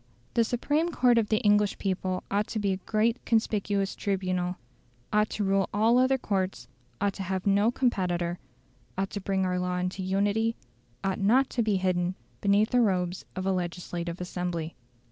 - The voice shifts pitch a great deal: No, average, 2.8 semitones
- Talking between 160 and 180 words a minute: Yes, average, 175 wpm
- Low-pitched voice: No, high, 195 Hz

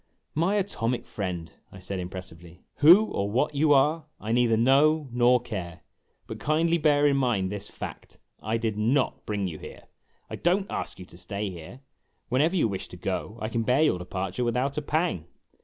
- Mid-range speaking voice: No, low, 120 Hz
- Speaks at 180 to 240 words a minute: Yes, average, 190 wpm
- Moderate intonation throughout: No, wide, 7.3 semitones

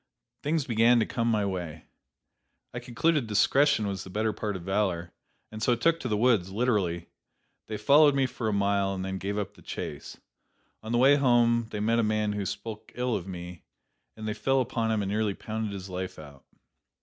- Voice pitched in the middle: No, low, 110 Hz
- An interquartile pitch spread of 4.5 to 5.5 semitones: No, average, 3.6 semitones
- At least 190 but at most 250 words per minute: Yes, fast, 205 wpm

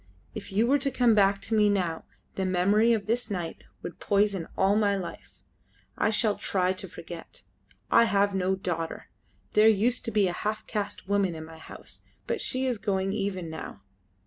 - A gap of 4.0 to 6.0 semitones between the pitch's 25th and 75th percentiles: No, narrow, 2.6 semitones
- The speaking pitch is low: No, high, 200 Hz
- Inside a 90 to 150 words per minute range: No, average, 190 wpm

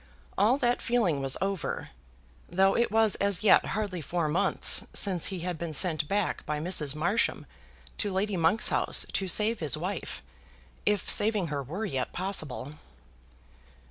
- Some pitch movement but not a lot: Yes, average, 4.7 semitones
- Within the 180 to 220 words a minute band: No, average, 155 wpm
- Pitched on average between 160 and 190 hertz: Yes, medium, 185 Hz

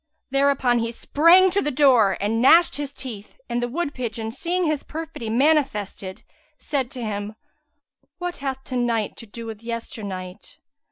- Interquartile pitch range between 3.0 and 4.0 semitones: No, average, 4.8 semitones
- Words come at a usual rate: Yes, average, 165 wpm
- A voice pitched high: Yes, high, 245 Hz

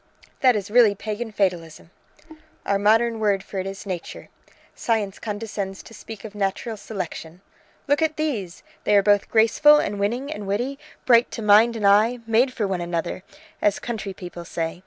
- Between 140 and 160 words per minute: No, average, 175 wpm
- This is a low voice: No, high, 210 Hz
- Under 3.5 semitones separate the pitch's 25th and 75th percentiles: Yes, average, 3.0 semitones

